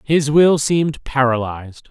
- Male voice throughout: Yes, male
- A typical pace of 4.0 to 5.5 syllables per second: Yes, 4.4 syllables/s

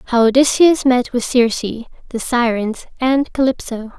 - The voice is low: No, high, 245 Hz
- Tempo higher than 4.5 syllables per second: No, 4.3 syllables/s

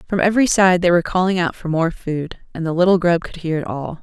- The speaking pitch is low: No, medium, 170 Hz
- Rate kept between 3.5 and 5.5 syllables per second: No, 6.2 syllables/s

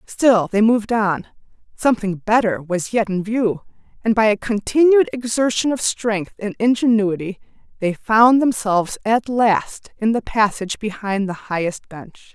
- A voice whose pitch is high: Yes, high, 215 Hz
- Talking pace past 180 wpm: No, average, 145 wpm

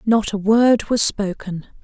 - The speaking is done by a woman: Yes, female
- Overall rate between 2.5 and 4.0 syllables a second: Yes, 3.8 syllables/s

